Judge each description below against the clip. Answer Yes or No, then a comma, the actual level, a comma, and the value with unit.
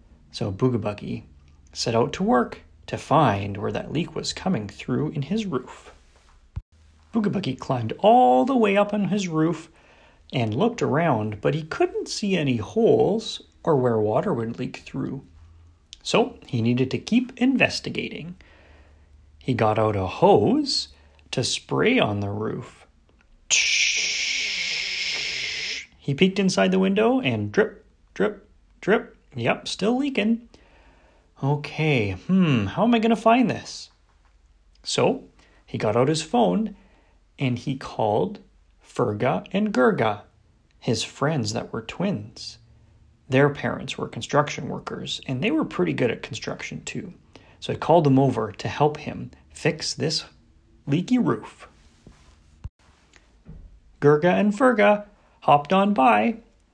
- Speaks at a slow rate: Yes, slow, 130 wpm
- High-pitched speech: No, low, 130 Hz